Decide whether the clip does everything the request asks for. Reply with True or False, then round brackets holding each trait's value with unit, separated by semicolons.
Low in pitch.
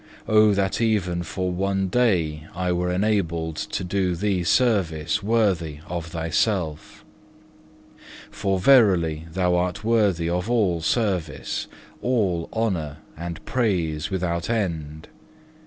True (90 Hz)